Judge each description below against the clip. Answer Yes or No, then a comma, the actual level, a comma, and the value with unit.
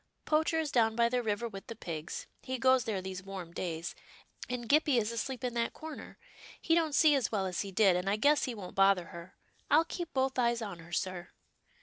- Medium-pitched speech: No, high, 230 Hz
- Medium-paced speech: No, fast, 225 wpm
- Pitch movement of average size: No, wide, 5.7 semitones